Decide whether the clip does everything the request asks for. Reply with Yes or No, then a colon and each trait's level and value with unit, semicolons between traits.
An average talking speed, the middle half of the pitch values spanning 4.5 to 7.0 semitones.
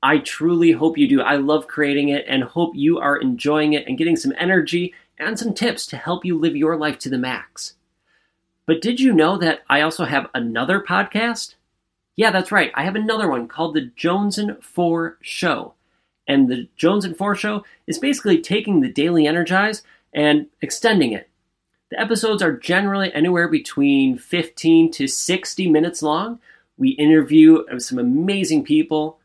Yes: average, 175 wpm; wide, 5.4 semitones